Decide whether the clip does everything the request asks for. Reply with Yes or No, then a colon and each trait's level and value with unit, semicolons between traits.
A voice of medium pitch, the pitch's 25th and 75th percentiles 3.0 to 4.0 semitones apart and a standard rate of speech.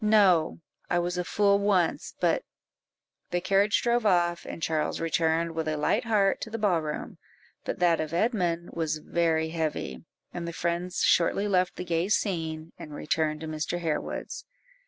Yes: medium, 170 Hz; average, 3.4 semitones; average, 175 wpm